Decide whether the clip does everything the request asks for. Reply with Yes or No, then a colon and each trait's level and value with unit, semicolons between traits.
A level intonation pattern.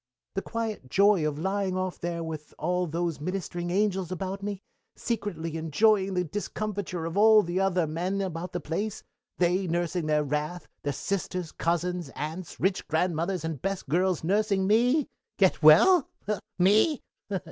No: average, 3.3 semitones